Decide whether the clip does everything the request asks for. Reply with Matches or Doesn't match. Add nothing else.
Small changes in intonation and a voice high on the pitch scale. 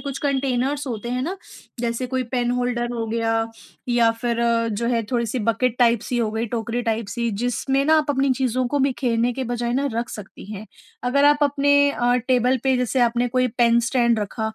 Matches